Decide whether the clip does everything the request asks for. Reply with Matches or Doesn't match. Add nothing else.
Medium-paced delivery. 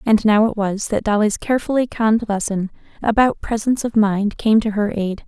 Matches